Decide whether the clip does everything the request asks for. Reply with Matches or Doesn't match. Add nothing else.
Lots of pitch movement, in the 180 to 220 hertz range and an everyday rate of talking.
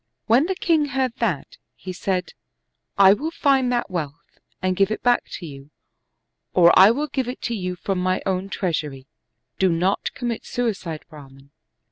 Matches